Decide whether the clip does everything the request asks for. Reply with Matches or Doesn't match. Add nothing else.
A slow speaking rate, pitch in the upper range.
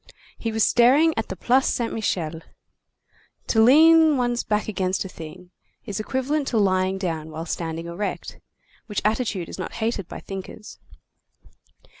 Doesn't match